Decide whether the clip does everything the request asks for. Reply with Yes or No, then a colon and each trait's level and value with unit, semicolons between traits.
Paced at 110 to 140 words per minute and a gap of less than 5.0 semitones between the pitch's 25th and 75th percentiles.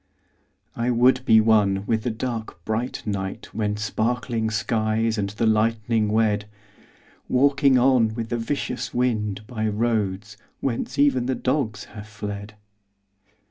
Yes: slow, 135 wpm; narrow, 2.5 semitones